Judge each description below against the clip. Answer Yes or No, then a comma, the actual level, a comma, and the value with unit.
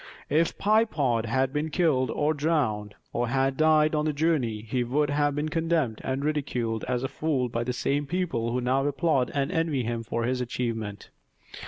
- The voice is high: No, low, 135 Hz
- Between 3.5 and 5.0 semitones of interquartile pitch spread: Yes, average, 4.2 semitones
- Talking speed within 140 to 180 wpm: No, average, 190 wpm